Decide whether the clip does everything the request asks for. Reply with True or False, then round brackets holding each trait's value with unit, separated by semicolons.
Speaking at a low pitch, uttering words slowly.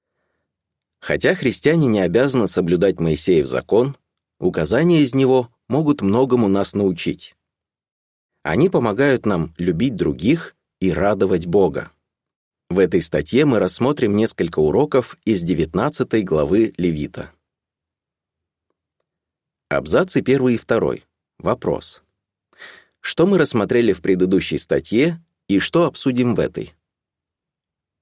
True (120 Hz; 105 wpm)